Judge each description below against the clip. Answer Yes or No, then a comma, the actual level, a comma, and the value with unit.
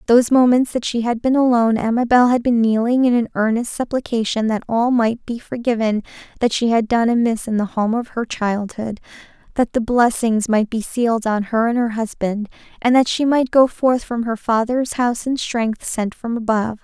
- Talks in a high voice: Yes, high, 235 Hz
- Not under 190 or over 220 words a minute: Yes, fast, 205 wpm